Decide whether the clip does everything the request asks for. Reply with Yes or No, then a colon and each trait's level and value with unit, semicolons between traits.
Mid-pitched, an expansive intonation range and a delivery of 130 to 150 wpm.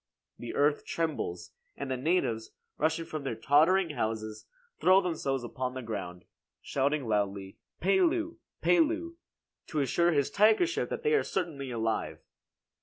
Yes: medium, 145 Hz; wide, 8.2 semitones; slow, 135 wpm